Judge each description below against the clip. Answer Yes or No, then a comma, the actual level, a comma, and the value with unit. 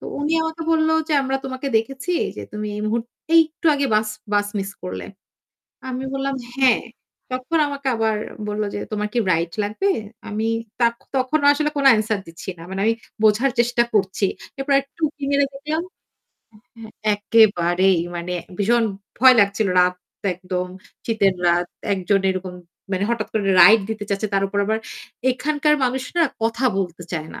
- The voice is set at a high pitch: Yes, high, 220 Hz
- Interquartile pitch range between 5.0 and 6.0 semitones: Yes, wide, 5.6 semitones